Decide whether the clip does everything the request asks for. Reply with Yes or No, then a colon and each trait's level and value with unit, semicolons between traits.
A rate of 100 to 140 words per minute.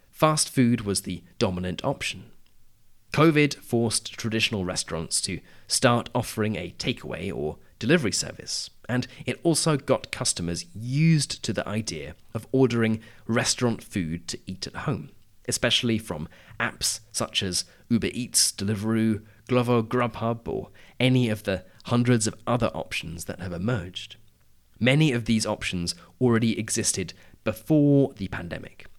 Yes: slow, 135 wpm